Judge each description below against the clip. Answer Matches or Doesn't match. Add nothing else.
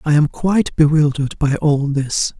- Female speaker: Doesn't match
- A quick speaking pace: Doesn't match